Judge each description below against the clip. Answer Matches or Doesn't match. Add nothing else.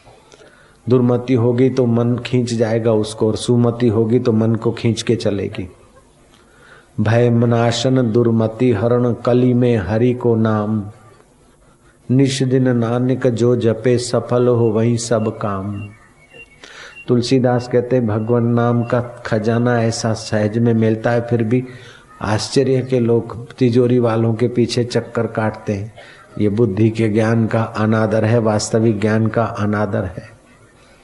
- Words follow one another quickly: Doesn't match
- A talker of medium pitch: Doesn't match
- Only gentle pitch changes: Matches